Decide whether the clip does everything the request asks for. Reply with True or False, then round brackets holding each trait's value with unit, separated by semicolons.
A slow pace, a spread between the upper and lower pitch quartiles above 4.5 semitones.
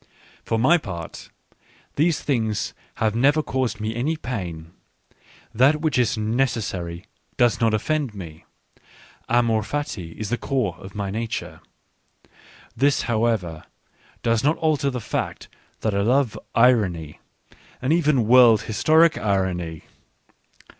True (125 wpm; 5.2 semitones)